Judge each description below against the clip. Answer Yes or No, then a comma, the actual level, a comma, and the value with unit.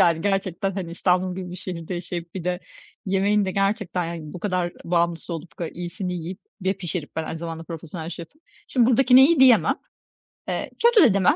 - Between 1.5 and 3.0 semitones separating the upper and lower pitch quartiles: Yes, average, 2.7 semitones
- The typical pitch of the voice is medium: Yes, medium, 180 Hz